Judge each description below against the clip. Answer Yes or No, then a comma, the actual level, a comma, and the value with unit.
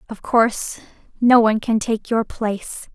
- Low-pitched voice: No, high, 225 Hz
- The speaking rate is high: No, average, 165 wpm